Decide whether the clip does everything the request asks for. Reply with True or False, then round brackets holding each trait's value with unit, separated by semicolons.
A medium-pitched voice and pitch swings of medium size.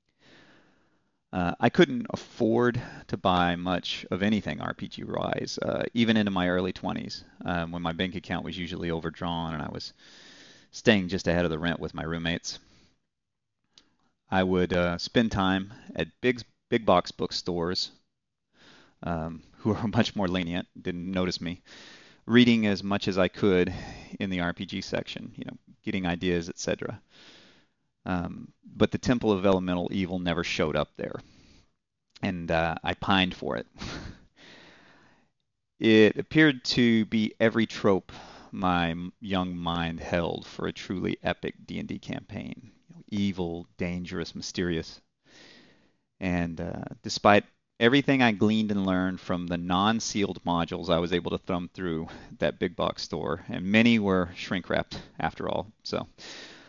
False (90 Hz; 3.6 semitones)